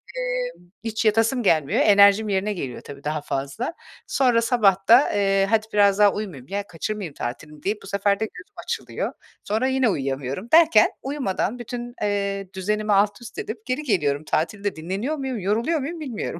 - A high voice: Yes, high, 205 Hz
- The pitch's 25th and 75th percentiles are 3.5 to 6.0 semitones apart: Yes, average, 4.0 semitones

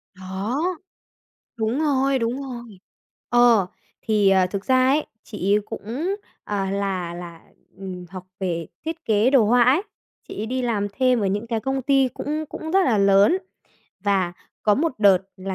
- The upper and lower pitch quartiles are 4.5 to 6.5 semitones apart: Yes, average, 5.1 semitones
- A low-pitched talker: No, high, 220 Hz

